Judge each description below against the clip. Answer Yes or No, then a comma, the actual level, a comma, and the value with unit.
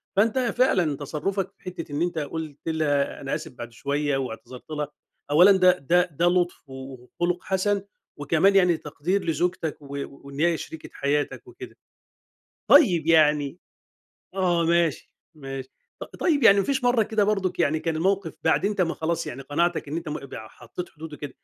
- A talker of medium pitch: Yes, medium, 165 Hz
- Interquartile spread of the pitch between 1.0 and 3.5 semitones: No, average, 4.2 semitones